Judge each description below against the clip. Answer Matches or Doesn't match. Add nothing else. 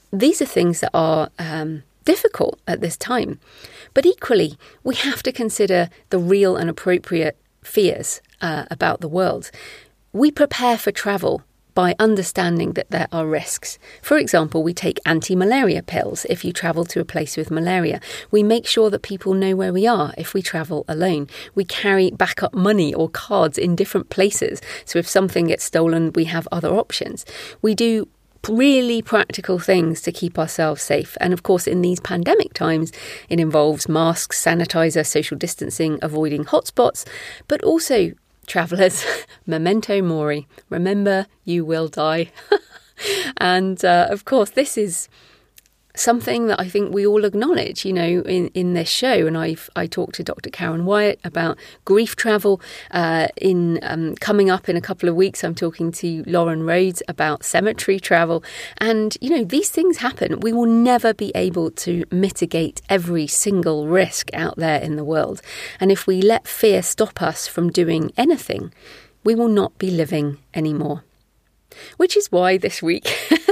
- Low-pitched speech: Doesn't match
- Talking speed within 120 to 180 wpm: Matches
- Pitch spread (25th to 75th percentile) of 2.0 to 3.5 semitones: Doesn't match